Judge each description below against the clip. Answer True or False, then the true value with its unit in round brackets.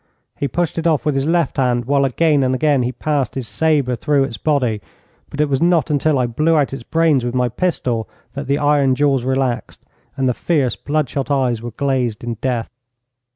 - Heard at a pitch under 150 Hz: True (135 Hz)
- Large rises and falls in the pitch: False (3.2 semitones)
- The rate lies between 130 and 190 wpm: False (205 wpm)